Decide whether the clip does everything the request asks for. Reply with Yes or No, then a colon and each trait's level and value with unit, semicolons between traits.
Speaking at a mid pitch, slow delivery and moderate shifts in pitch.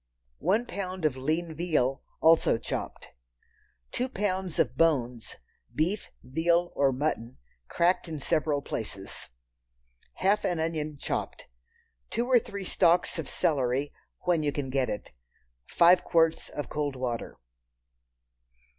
Yes: medium, 160 Hz; slow, 120 wpm; average, 4.5 semitones